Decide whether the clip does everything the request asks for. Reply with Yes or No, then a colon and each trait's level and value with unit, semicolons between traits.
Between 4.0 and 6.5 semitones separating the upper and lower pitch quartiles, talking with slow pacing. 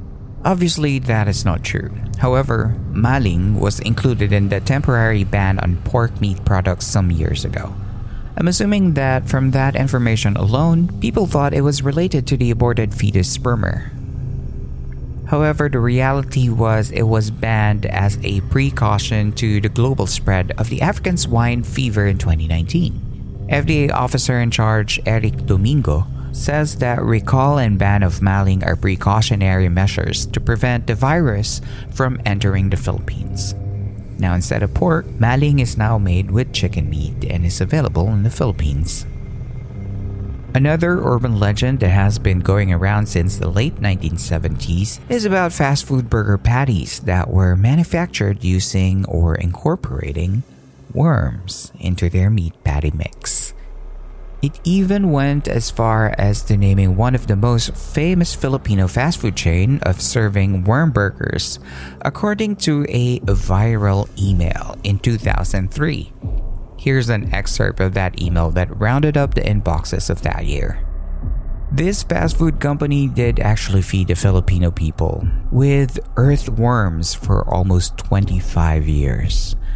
No: average, 5.1 semitones; average, 140 wpm